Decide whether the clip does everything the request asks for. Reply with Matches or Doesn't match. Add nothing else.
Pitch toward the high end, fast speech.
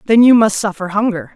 Matches